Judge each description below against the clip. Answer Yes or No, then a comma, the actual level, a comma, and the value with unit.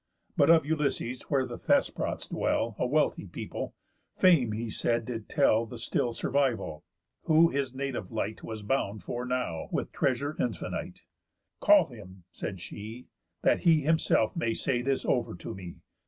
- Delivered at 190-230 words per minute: No, average, 155 wpm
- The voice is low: Yes, low, 125 Hz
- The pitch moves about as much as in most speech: Yes, average, 4.2 semitones